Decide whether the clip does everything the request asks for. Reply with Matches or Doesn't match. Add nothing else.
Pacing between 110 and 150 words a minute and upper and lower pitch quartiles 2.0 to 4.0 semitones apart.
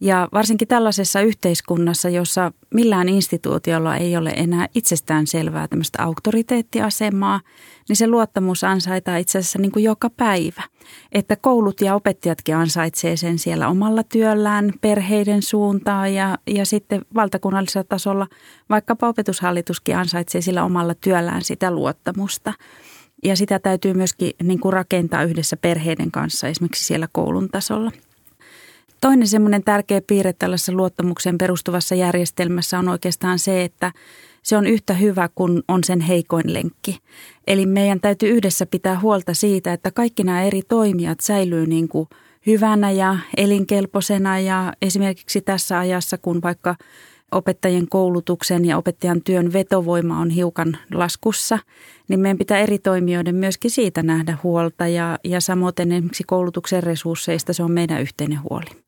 Matches